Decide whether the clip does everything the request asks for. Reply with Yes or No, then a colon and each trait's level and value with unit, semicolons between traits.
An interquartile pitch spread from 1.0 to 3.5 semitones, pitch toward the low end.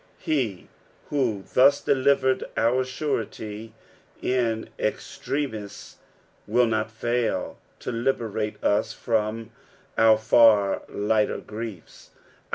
Yes: average, 2.9 semitones; low, 115 Hz